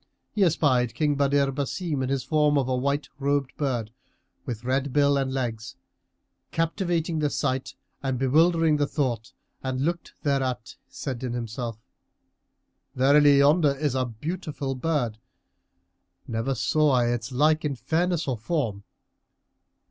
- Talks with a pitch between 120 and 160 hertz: Yes, medium, 140 Hz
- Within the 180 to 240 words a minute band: No, average, 140 wpm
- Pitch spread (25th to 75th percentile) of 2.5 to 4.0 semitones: Yes, average, 3.1 semitones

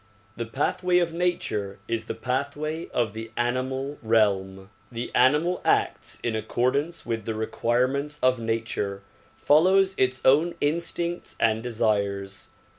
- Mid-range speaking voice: No, low, 125 Hz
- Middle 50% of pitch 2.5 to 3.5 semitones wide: No, average, 5.0 semitones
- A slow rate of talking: Yes, slow, 130 wpm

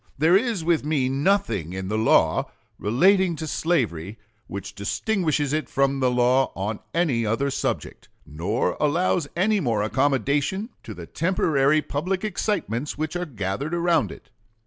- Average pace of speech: Yes, average, 145 wpm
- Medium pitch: Yes, medium, 145 Hz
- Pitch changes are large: Yes, wide, 6.9 semitones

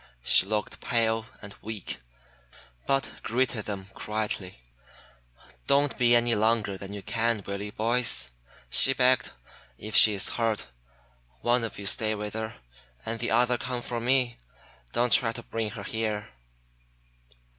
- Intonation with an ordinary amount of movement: No, narrow, 2.3 semitones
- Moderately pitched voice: No, low, 115 Hz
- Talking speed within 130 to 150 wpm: Yes, average, 145 wpm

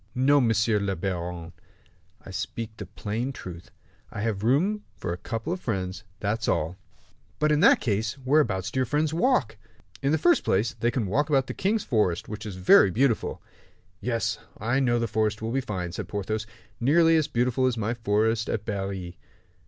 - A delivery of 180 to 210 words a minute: Yes, average, 185 wpm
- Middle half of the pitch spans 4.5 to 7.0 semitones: Yes, average, 4.8 semitones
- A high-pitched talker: No, low, 115 Hz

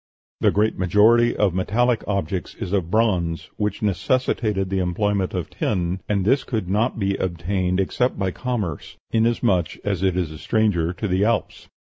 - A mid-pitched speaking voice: No, low, 100 Hz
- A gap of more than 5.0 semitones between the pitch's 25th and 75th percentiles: No, average, 3.3 semitones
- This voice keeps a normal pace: Yes, average, 165 wpm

